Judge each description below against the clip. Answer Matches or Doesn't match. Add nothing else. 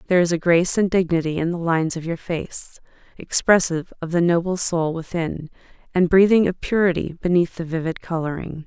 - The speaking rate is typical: Matches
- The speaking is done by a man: Doesn't match